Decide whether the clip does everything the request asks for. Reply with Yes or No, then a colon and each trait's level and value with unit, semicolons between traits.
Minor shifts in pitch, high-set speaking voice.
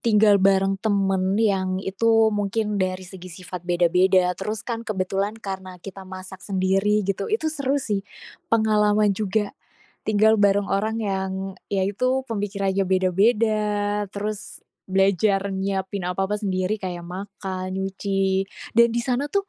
Yes: narrow, 2.1 semitones; high, 195 Hz